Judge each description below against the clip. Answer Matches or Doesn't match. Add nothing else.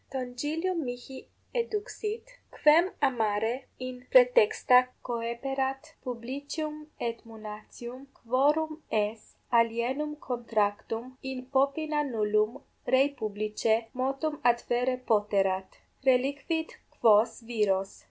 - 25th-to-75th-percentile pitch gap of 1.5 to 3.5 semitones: Doesn't match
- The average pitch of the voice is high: Matches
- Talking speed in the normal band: Doesn't match